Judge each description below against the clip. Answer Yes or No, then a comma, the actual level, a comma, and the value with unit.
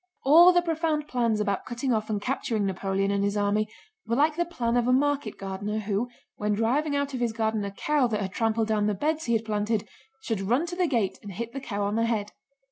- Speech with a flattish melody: No, average, 4.8 semitones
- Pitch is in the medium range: No, high, 225 Hz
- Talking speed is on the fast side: Yes, fast, 240 wpm